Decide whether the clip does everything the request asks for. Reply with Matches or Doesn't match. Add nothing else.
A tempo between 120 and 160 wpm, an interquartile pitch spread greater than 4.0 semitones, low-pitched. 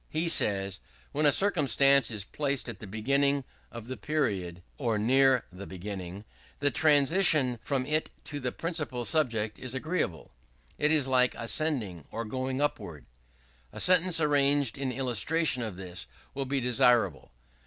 Matches